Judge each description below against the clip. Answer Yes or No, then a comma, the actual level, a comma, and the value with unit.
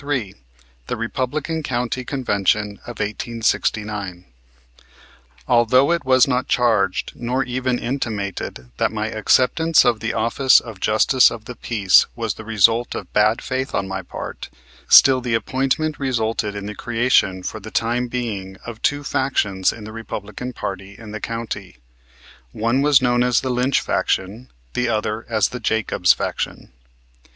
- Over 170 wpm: No, average, 155 wpm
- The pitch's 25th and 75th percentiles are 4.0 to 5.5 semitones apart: No, average, 3.3 semitones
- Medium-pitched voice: No, low, 115 Hz